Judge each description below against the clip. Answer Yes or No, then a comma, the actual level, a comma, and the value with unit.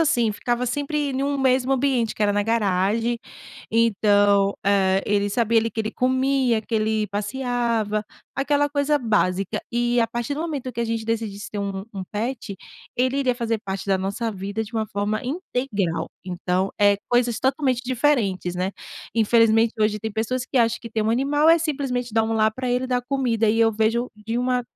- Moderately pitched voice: No, high, 230 Hz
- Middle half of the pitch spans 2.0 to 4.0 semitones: Yes, average, 3.4 semitones